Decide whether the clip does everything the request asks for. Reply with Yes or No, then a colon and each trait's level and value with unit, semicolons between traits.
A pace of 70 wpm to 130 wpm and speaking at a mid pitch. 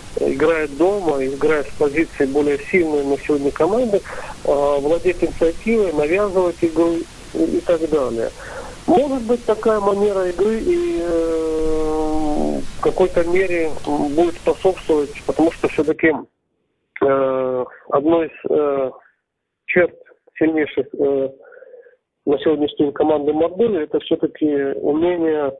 Yes: slow, 110 wpm; medium, 160 Hz